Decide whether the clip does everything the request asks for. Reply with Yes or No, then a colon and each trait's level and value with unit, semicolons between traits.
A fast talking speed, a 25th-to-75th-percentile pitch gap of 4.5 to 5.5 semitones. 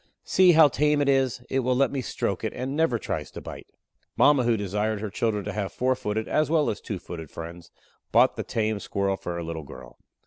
Yes: fast, 230 wpm; average, 5.2 semitones